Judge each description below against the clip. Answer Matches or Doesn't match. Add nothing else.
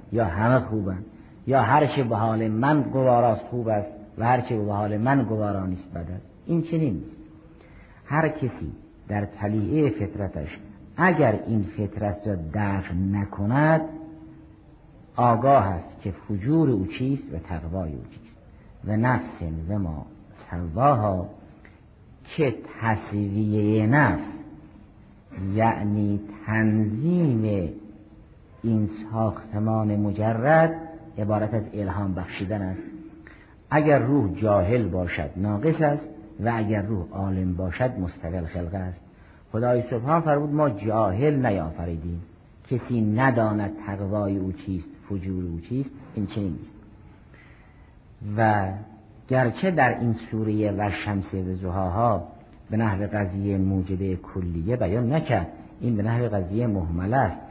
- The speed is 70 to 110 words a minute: Doesn't match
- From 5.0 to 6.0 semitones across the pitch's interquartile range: Doesn't match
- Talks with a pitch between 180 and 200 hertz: Doesn't match